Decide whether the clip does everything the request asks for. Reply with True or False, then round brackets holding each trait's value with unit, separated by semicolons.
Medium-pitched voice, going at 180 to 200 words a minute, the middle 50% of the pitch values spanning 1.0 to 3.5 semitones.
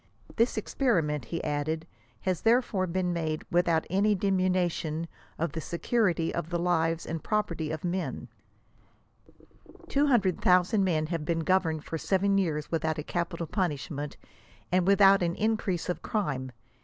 False (175 Hz; 165 wpm; 3.2 semitones)